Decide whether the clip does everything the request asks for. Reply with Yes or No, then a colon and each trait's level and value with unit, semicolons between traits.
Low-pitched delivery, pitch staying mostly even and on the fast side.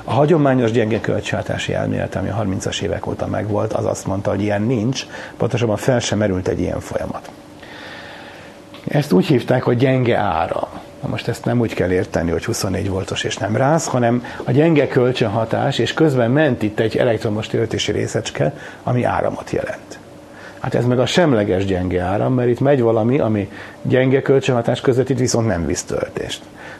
No: low, 115 Hz; average, 3.8 semitones; fast, 175 wpm